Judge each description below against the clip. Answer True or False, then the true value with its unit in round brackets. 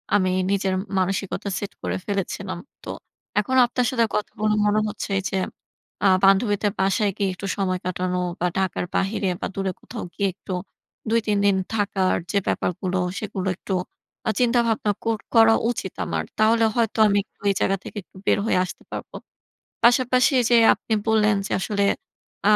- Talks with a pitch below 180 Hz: False (205 Hz)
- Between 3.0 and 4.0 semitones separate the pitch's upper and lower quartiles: False (2.5 semitones)